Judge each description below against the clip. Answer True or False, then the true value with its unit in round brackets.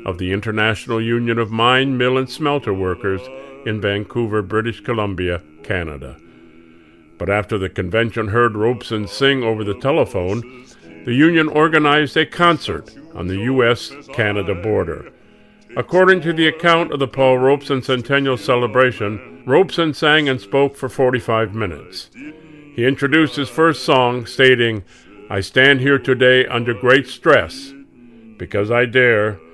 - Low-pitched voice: True (120 Hz)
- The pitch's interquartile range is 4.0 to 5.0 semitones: True (4.6 semitones)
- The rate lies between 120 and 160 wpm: True (140 wpm)